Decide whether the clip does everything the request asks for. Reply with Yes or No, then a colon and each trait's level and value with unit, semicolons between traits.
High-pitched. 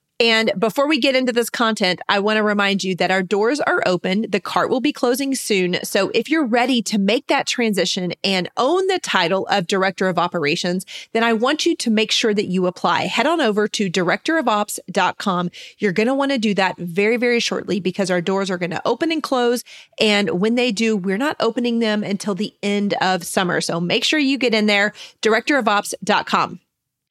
Yes: high, 210 Hz